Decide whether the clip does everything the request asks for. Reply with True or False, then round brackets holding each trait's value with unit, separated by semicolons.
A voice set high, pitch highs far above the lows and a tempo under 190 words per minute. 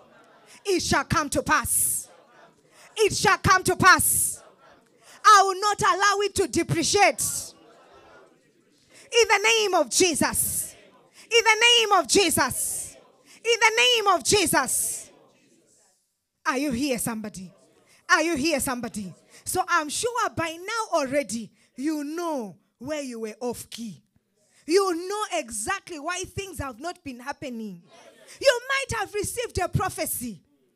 True (330 Hz; 6.7 semitones; 135 wpm)